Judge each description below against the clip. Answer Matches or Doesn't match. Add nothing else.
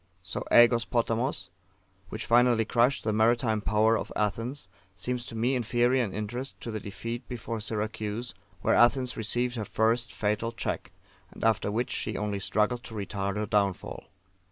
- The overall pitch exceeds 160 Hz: Doesn't match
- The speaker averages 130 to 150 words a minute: Doesn't match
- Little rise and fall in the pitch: Matches